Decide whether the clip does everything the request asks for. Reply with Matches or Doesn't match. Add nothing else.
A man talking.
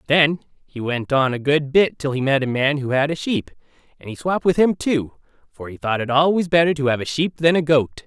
Matches